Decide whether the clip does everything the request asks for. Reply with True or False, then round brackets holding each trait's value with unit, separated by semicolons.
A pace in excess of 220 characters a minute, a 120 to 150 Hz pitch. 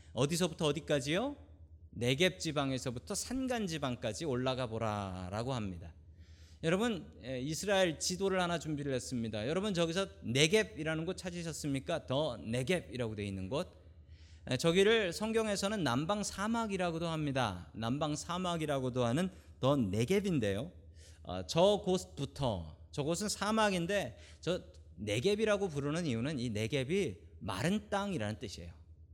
True (315 characters per minute; 140 Hz)